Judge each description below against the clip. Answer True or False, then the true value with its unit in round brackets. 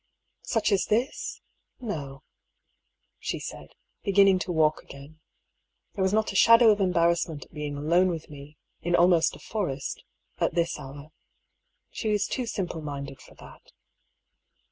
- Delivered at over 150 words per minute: False (145 wpm)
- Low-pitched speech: False (170 Hz)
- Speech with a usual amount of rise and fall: True (5.0 semitones)